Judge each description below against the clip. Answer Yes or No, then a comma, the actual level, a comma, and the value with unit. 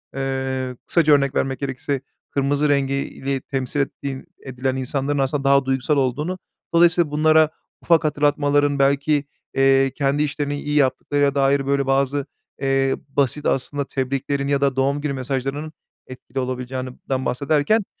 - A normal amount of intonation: No, narrow, 1.4 semitones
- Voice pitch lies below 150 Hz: Yes, medium, 140 Hz